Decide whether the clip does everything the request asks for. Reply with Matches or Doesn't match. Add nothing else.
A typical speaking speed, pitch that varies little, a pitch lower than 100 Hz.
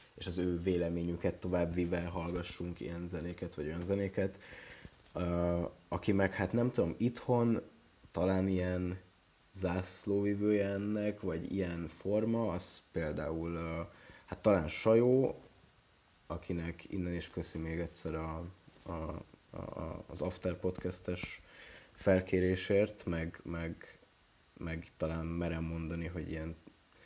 Matches